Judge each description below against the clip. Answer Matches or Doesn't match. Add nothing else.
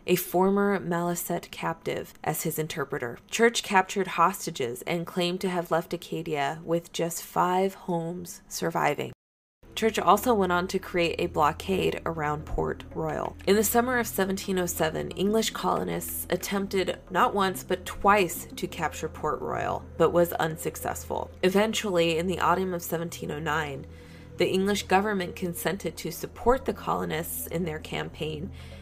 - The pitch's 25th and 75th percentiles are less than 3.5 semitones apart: Matches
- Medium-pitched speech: Matches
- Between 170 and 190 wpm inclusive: Doesn't match